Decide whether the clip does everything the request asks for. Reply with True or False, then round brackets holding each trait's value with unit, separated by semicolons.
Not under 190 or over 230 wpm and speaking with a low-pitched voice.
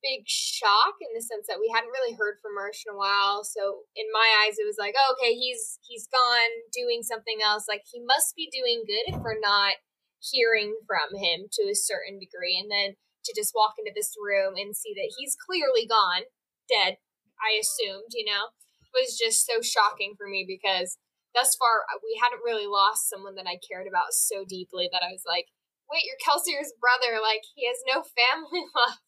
False (205 wpm; 230 Hz)